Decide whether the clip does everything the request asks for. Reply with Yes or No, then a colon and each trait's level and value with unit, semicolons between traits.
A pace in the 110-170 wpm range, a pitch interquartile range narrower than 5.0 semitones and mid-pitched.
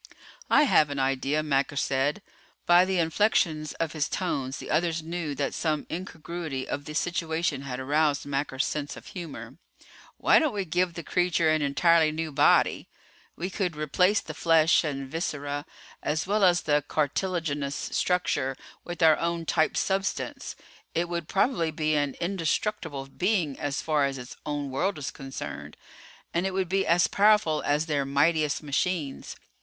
Yes: average, 160 wpm; average, 3.4 semitones; medium, 155 Hz